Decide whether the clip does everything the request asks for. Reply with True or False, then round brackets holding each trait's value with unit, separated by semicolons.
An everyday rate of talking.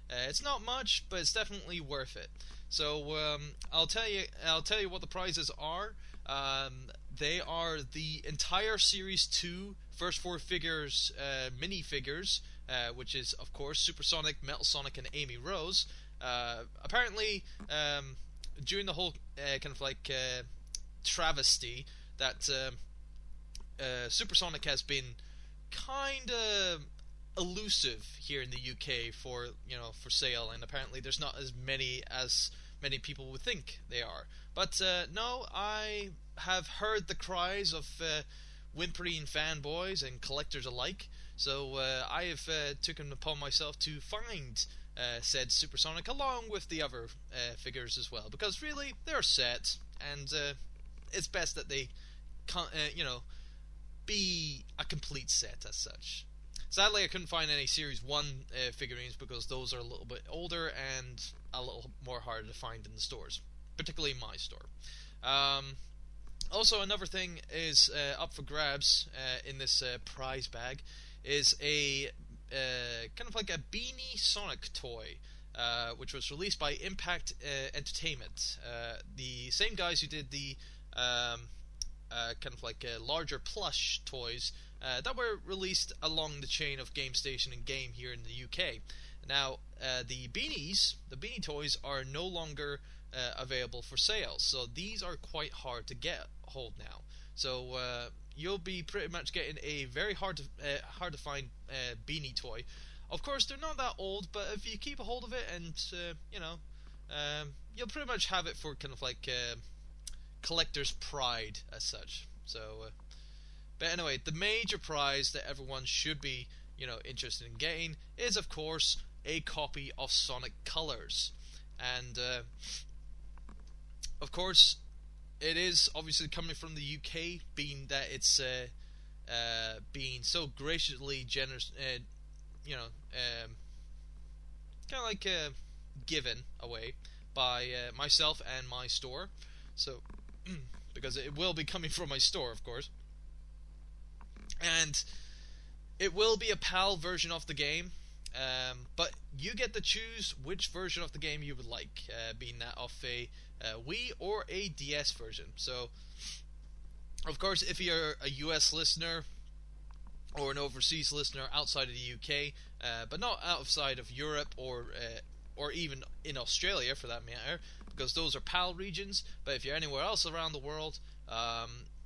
True (160 wpm)